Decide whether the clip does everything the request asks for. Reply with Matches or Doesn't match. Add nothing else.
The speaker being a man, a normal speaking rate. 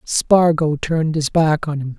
Matches